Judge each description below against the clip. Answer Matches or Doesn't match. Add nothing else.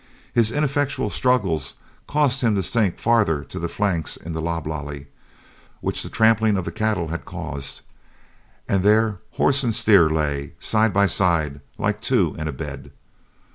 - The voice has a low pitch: Matches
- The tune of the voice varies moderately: Doesn't match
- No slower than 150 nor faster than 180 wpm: Matches